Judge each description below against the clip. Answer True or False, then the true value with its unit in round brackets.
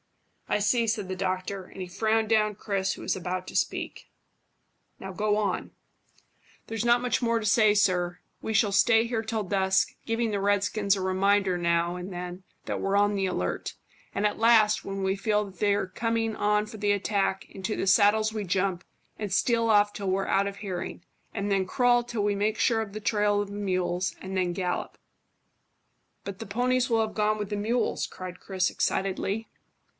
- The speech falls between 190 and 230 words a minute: True (195 wpm)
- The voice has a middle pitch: False (205 Hz)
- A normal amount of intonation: False (2.3 semitones)